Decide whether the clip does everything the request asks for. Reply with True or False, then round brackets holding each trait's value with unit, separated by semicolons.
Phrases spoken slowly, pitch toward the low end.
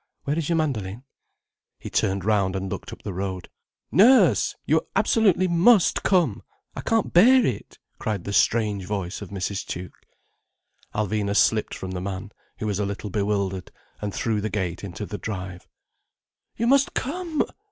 False (165 wpm; 105 Hz)